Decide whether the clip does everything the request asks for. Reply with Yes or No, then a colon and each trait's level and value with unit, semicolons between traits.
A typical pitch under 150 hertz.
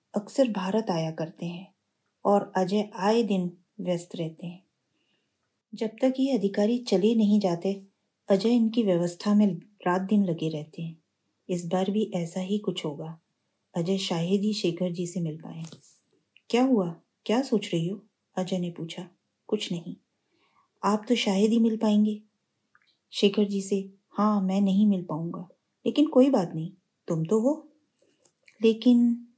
No: high, 200 Hz